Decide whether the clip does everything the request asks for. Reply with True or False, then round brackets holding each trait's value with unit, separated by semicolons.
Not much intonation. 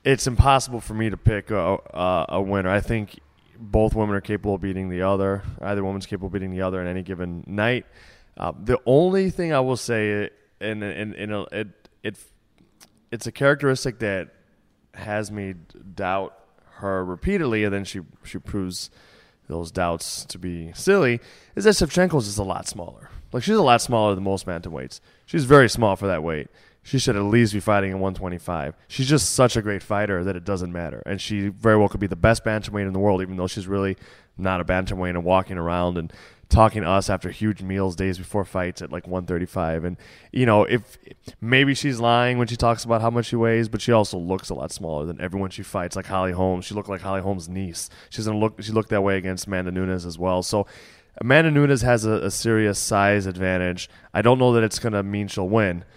False (3.2 semitones)